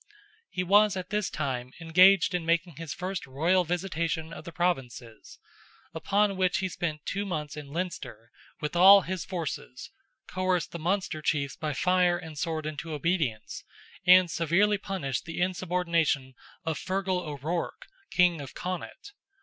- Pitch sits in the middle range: Yes, medium, 170 Hz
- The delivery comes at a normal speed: Yes, average, 150 wpm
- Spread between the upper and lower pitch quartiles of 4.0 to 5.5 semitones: No, average, 3.3 semitones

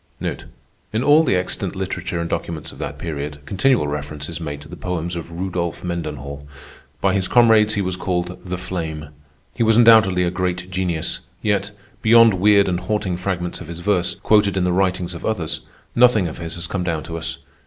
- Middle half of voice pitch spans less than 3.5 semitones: Yes, average, 3.0 semitones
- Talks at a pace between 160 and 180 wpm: No, average, 195 wpm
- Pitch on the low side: Yes, very low, 90 Hz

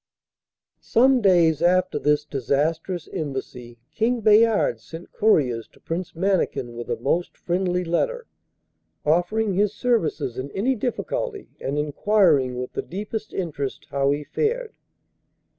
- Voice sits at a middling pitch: Yes, medium, 175 Hz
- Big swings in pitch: Yes, wide, 6.9 semitones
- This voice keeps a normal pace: No, slow, 125 wpm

